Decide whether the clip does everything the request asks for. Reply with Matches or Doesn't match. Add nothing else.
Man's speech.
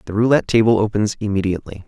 Matches